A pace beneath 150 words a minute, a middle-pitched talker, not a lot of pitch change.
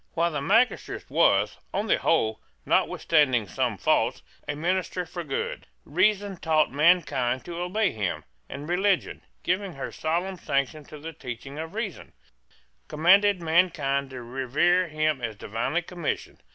No: average, 140 wpm; medium, 160 Hz; average, 4.7 semitones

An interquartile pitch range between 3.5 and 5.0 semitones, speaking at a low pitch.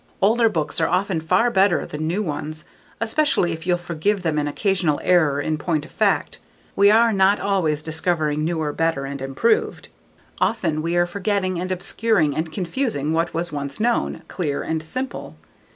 No: average, 4.3 semitones; medium, 170 Hz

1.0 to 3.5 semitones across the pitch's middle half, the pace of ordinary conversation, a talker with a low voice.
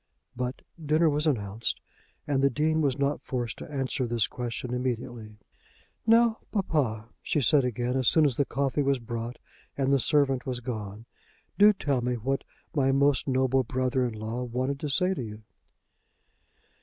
Yes: average, 2.9 semitones; average, 170 wpm; low, 130 Hz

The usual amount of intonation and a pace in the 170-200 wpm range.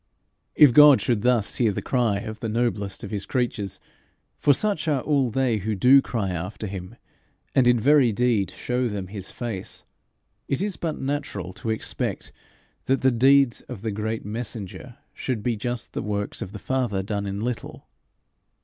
Yes: average, 4.1 semitones; average, 175 wpm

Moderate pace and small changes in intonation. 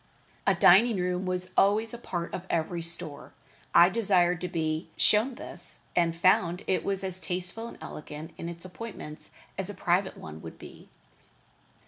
Yes: average, 160 wpm; narrow, 2.3 semitones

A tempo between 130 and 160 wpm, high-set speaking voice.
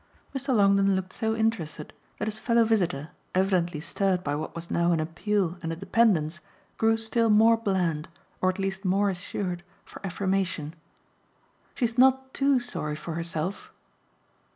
Yes: average, 155 wpm; high, 195 Hz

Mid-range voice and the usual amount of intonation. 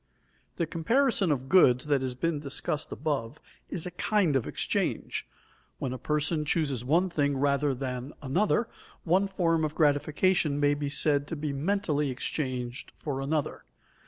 Yes: medium, 150 Hz; average, 3.5 semitones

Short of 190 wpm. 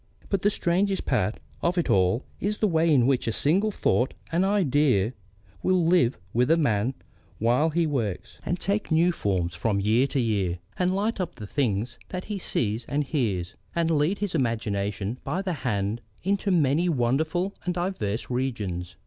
Yes: average, 175 wpm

